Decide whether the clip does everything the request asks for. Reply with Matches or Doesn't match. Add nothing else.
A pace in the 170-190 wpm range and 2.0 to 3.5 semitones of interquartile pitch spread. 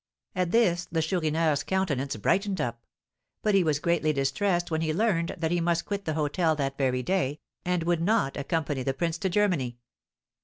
Doesn't match